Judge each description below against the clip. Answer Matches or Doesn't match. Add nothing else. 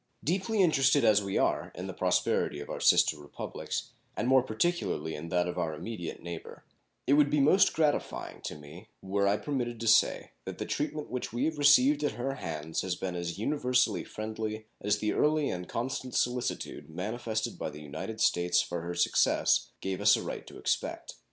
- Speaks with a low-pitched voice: Matches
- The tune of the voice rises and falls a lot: Matches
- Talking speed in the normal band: Matches